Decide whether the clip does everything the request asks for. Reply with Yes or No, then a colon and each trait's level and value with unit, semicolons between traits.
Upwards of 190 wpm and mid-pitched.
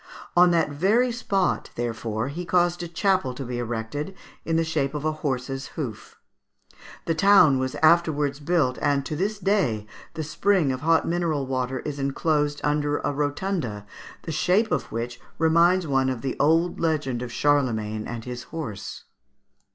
No: average, 165 wpm; medium, 145 Hz